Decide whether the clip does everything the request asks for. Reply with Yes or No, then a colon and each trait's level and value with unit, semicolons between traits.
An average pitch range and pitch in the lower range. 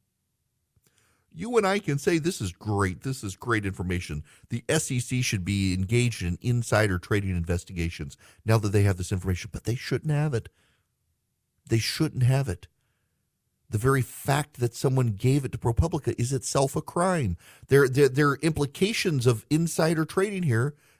No: wide, 6.2 semitones; low, 120 Hz